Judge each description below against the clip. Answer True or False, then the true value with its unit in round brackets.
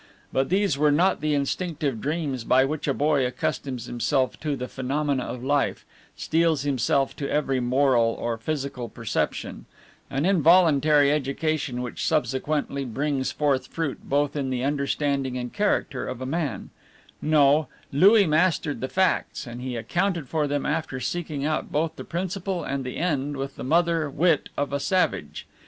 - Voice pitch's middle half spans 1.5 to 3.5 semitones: True (3.0 semitones)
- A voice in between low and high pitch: True (145 Hz)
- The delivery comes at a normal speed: True (160 wpm)